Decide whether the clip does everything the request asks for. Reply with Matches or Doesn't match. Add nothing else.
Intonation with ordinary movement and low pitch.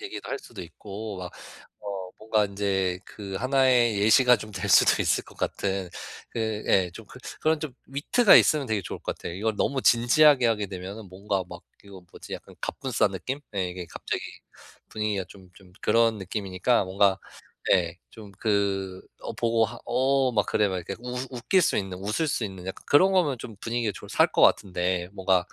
Matches